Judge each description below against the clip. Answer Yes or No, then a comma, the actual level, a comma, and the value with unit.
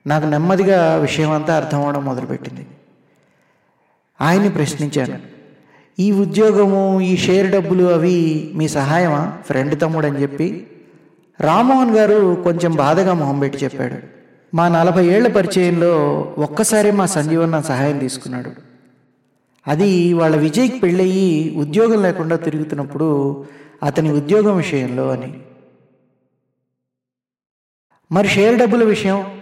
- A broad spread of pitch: No, average, 5.0 semitones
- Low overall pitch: No, medium, 160 Hz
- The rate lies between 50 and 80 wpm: No, average, 105 wpm